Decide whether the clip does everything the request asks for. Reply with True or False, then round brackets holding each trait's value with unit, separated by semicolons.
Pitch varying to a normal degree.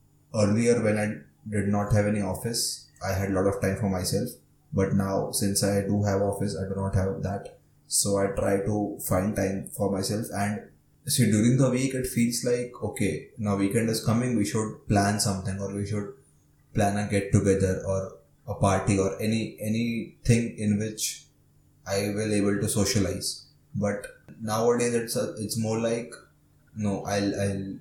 False (2.2 semitones)